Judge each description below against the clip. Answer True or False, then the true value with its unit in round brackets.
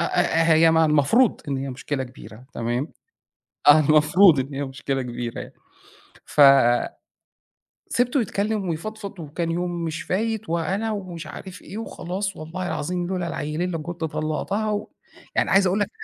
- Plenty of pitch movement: False (4.7 semitones)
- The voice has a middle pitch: True (165 Hz)